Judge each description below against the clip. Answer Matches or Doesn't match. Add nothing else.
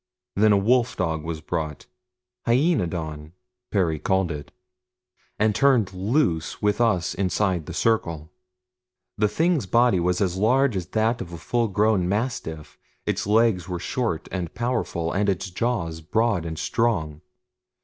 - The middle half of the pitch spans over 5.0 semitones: Matches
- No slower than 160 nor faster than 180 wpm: Doesn't match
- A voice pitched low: Matches